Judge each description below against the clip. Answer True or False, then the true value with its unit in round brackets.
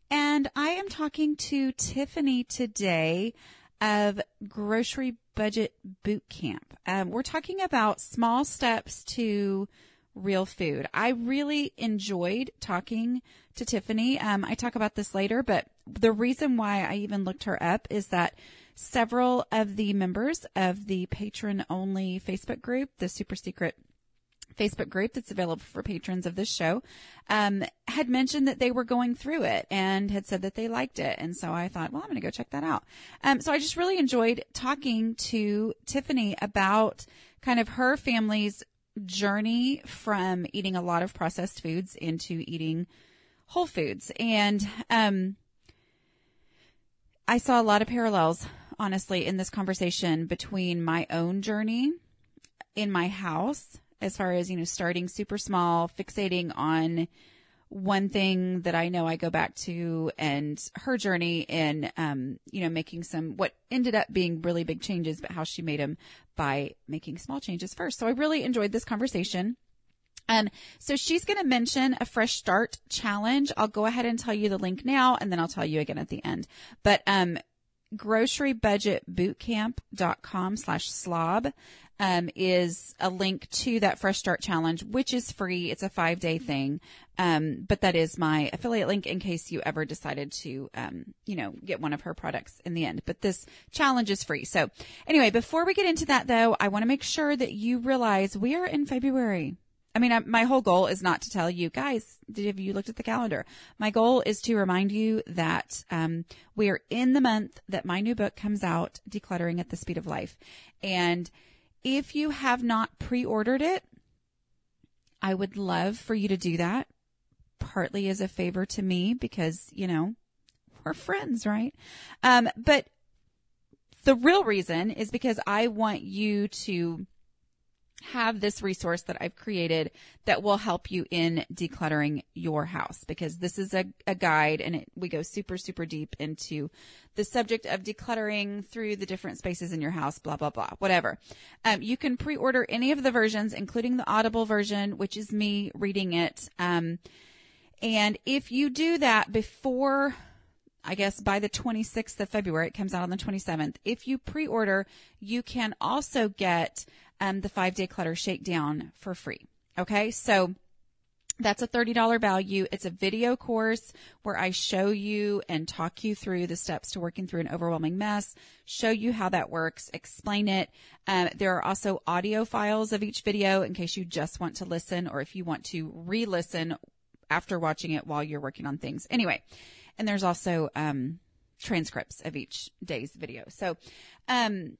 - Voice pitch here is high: True (200 Hz)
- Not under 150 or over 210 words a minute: True (175 wpm)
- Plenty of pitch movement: False (4.7 semitones)